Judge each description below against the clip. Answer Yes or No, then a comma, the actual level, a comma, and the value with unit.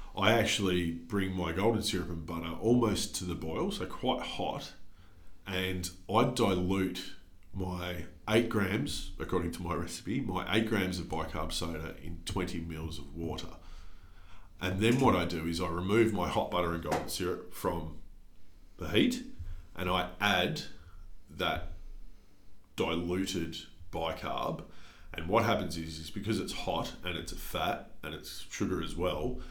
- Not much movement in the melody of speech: Yes, narrow, 2.2 semitones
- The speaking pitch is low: Yes, very low, 90 Hz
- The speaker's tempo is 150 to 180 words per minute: Yes, average, 155 wpm